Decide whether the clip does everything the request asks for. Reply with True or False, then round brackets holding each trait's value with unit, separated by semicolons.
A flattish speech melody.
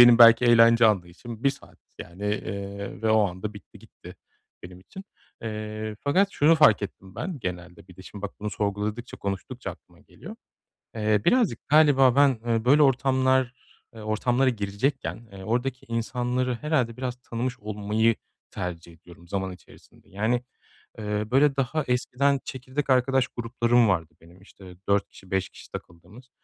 False (4.3 semitones)